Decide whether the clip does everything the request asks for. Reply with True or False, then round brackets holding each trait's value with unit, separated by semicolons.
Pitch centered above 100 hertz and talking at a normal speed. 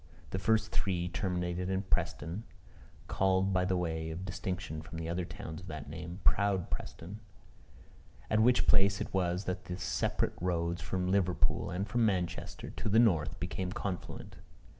False (90 Hz; 155 wpm)